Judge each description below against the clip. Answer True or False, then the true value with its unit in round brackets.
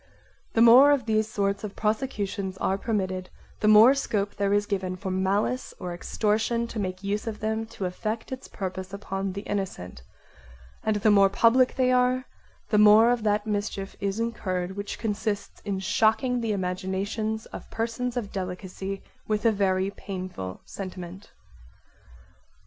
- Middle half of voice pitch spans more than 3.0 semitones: False (2.6 semitones)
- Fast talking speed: False (155 wpm)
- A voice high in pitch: True (205 Hz)